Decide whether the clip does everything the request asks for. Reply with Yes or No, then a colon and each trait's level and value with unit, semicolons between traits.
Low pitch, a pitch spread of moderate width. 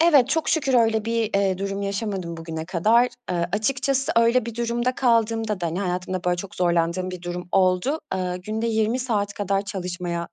No: high, 200 Hz; average, 4.4 semitones